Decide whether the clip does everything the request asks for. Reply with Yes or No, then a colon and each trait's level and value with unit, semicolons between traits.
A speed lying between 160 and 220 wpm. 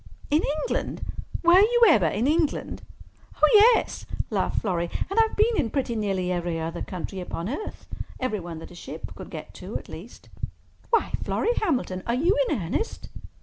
Yes: average, 170 wpm